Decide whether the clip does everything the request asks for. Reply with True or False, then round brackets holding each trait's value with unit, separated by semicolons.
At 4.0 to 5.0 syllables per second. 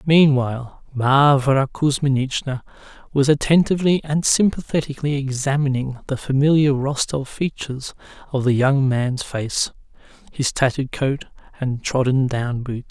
True (4.7 syllables/s)